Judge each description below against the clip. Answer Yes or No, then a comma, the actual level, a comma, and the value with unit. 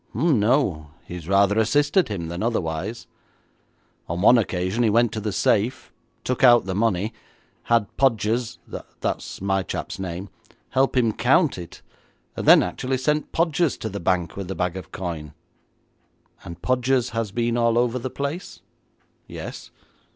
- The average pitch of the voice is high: No, low, 110 Hz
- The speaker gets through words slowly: No, average, 160 wpm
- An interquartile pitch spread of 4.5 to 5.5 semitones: Yes, average, 5.0 semitones